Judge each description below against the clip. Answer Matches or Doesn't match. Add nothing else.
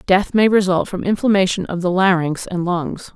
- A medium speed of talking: Matches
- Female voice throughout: Matches